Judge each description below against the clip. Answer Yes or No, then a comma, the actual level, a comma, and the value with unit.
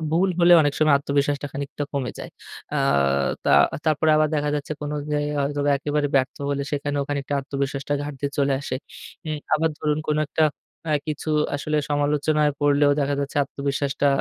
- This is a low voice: No, medium, 145 Hz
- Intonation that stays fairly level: Yes, narrow, 1.1 semitones